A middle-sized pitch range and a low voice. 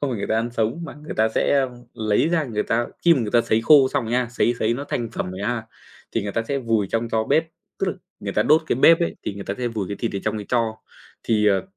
Yes: average, 3.6 semitones; low, 115 Hz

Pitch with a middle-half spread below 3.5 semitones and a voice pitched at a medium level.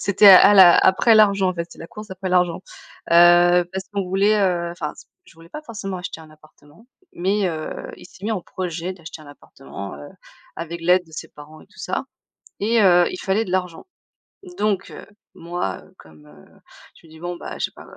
Yes: average, 2.7 semitones; medium, 180 Hz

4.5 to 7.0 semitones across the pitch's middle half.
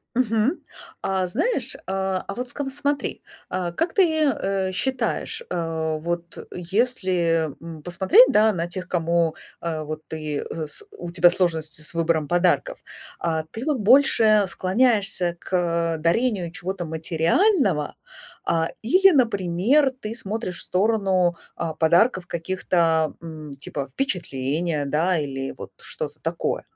Yes: average, 5.0 semitones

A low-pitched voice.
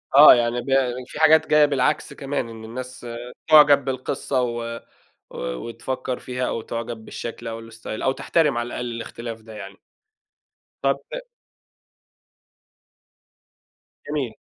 Yes: low, 125 Hz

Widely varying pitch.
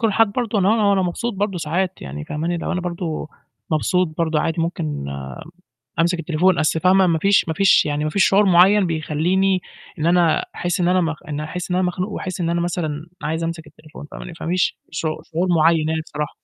No: average, 3.0 semitones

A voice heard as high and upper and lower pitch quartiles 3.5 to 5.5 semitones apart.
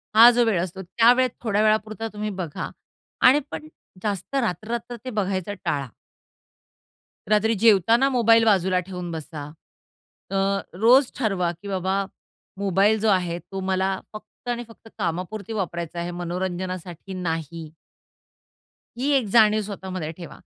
Yes: high, 195 Hz; average, 3.8 semitones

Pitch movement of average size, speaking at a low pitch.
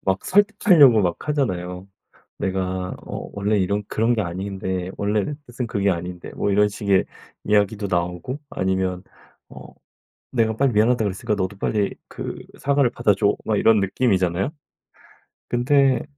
Yes: average, 4.1 semitones; low, 100 Hz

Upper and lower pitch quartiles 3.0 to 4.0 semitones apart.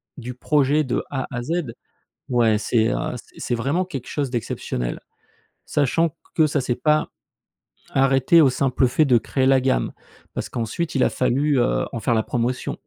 Yes: average, 3.3 semitones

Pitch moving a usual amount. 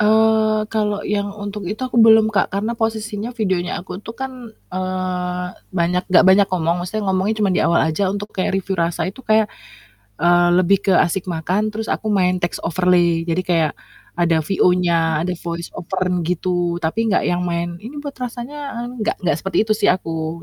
Yes: average, 3.6 semitones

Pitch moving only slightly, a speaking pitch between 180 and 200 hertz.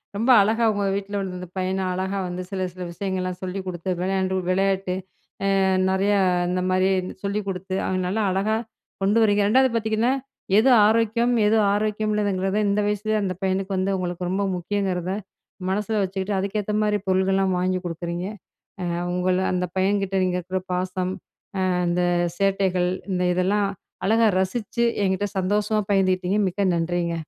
Yes: narrow, 2.0 semitones; high, 190 Hz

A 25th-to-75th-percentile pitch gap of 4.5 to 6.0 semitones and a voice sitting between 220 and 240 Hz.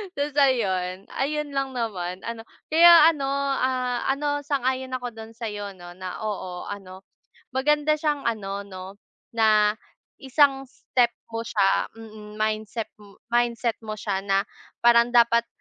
Yes: average, 4.8 semitones; high, 230 Hz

